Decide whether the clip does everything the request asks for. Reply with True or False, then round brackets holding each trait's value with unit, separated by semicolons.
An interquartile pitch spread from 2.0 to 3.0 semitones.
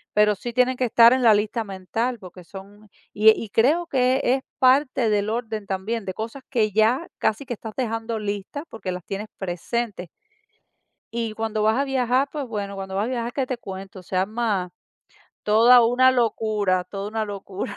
False (3.4 semitones)